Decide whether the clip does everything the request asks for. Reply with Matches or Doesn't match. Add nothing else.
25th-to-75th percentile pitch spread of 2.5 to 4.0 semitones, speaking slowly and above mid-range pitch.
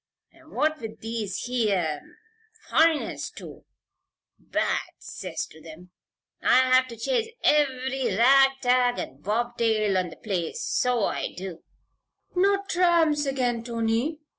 Doesn't match